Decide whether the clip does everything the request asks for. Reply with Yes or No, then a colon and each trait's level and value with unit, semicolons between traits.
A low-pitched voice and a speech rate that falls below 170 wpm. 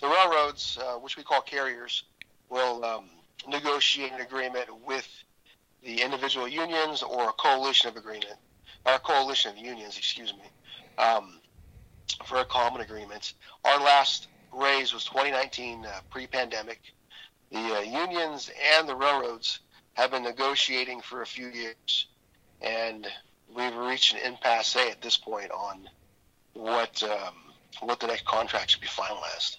Yes: low, 125 Hz; average, 145 wpm